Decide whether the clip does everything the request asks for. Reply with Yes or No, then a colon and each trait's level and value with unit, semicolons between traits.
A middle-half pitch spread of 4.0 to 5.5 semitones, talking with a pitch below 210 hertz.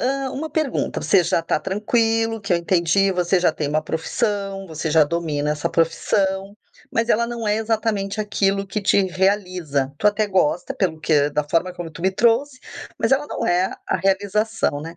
Yes: average, 4.4 semitones; high, 195 Hz